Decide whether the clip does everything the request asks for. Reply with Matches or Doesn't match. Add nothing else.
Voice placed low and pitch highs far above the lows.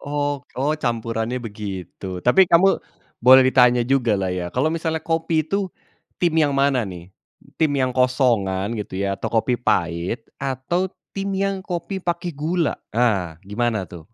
Matches